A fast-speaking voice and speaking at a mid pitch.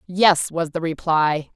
No: average, 155 wpm; medium, 165 Hz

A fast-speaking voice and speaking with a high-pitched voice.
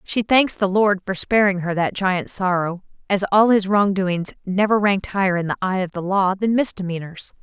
Yes: fast, 210 wpm; high, 195 Hz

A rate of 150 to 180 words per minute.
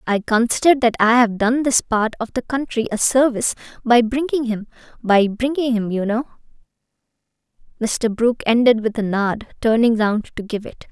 Yes: average, 170 wpm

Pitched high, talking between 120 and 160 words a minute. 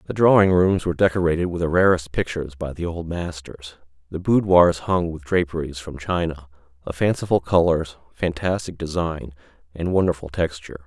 No: very low, 85 Hz; average, 155 wpm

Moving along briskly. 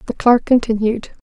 No: average, 145 wpm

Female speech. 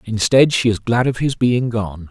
No: male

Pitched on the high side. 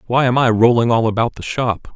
No: low, 120 Hz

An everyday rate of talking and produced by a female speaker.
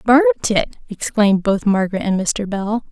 Yes: average, 165 wpm; female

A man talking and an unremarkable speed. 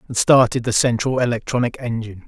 Yes: male; average, 160 wpm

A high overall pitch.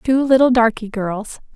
Yes: high, 230 Hz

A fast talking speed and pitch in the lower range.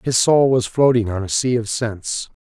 Yes: fast, 220 wpm; low, 120 Hz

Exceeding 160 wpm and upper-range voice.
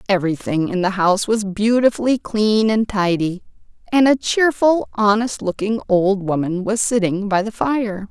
No: average, 155 wpm; high, 210 Hz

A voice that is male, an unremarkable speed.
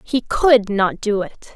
No: female; average, 195 wpm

